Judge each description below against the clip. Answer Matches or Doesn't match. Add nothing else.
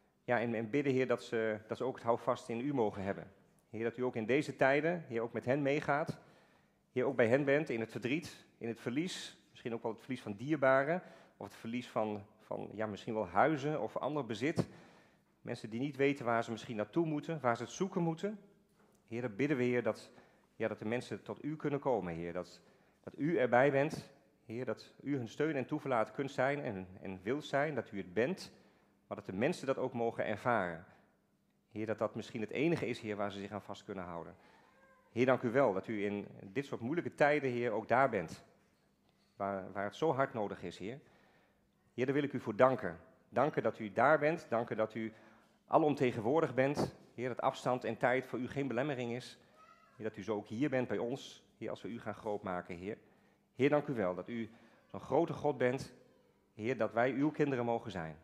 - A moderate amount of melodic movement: Matches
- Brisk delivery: Matches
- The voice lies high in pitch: Doesn't match